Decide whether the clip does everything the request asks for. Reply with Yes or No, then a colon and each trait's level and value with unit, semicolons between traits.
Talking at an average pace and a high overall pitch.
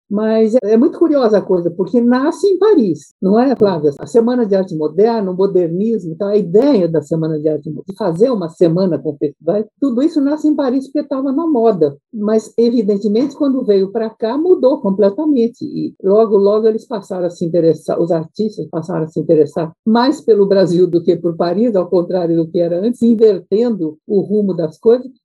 No: fast, 195 wpm; high, 210 Hz